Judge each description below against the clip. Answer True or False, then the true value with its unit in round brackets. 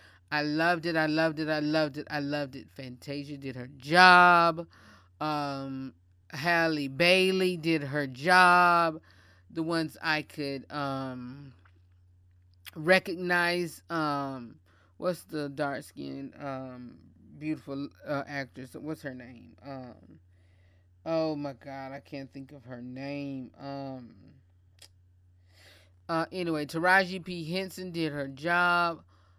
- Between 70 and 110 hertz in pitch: False (140 Hz)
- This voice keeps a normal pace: False (120 wpm)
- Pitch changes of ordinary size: False (6.1 semitones)